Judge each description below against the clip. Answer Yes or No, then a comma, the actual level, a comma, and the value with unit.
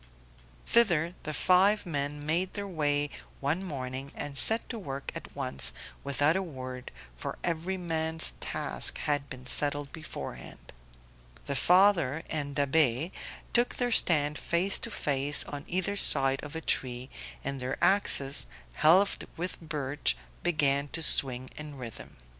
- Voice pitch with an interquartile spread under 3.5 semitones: No, average, 4.1 semitones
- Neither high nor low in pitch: Yes, medium, 150 Hz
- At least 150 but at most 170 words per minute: No, average, 140 wpm